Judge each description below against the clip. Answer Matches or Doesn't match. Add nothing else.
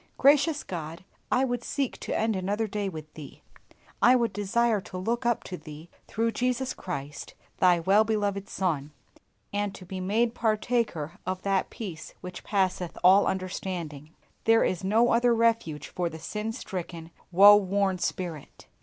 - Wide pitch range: Doesn't match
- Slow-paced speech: Doesn't match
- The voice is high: Matches